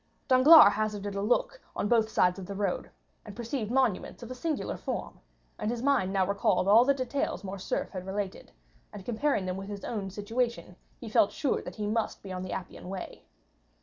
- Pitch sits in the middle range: No, high, 210 Hz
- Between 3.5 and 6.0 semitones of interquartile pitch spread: Yes, average, 3.9 semitones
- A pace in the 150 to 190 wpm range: No, average, 200 wpm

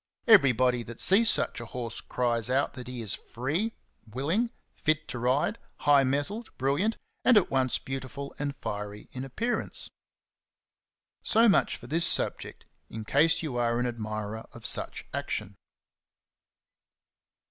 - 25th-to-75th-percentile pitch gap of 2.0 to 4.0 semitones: No, average, 5.1 semitones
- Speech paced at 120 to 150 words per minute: Yes, average, 140 wpm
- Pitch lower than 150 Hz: Yes, low, 135 Hz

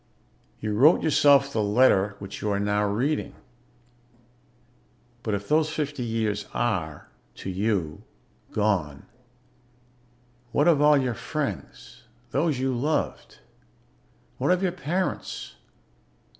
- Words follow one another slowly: Yes, slow, 115 wpm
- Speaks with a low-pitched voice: Yes, low, 120 Hz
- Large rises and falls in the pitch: Yes, wide, 6.2 semitones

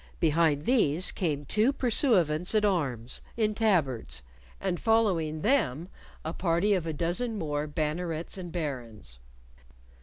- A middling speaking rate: No, slow, 125 wpm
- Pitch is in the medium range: Yes, medium, 165 Hz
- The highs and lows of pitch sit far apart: Yes, wide, 5.8 semitones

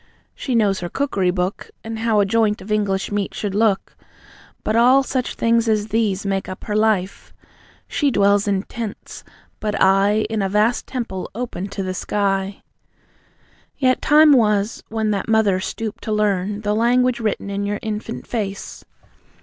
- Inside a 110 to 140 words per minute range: No, average, 165 wpm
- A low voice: No, high, 210 Hz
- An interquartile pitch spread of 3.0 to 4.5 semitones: No, narrow, 2.4 semitones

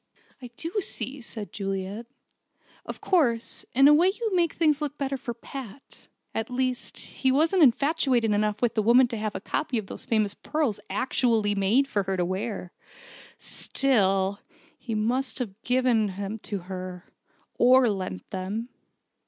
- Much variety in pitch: No, average, 4.9 semitones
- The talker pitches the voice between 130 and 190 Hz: No, high, 235 Hz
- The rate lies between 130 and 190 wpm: Yes, average, 160 wpm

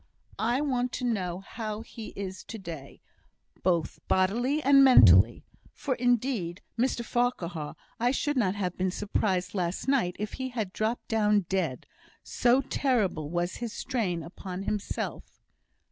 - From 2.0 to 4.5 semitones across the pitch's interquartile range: No, average, 5.3 semitones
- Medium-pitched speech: No, high, 210 Hz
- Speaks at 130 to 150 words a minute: Yes, average, 145 wpm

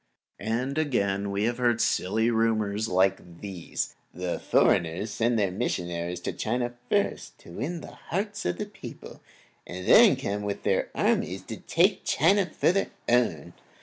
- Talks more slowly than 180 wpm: Yes, average, 150 wpm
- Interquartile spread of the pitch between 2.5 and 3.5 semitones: No, average, 4.7 semitones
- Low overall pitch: Yes, low, 110 Hz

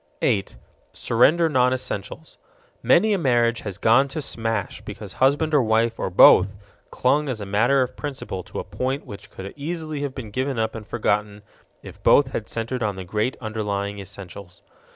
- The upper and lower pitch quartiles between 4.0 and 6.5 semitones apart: Yes, average, 4.8 semitones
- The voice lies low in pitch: Yes, low, 115 Hz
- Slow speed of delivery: No, average, 175 wpm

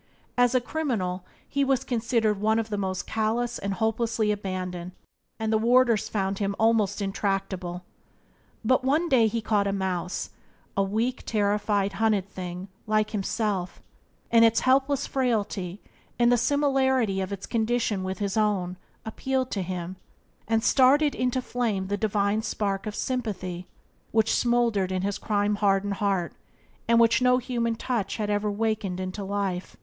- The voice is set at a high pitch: Yes, high, 215 Hz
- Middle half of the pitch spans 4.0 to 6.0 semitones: No, average, 3.3 semitones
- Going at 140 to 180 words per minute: Yes, average, 160 wpm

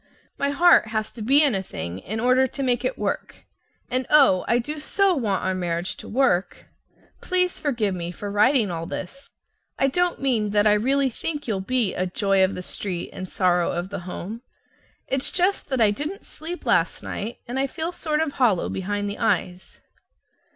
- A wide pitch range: Yes, wide, 6.6 semitones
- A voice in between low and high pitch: No, high, 230 Hz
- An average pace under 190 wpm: No, average, 195 wpm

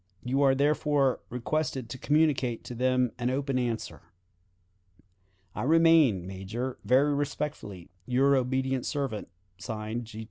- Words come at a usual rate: No, slow, 130 wpm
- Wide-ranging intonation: No, average, 3.1 semitones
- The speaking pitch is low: Yes, low, 130 Hz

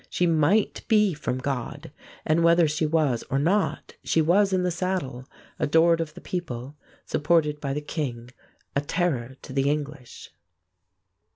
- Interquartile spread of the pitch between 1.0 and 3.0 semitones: No, average, 3.8 semitones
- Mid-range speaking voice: Yes, medium, 155 Hz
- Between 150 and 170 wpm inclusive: Yes, average, 155 wpm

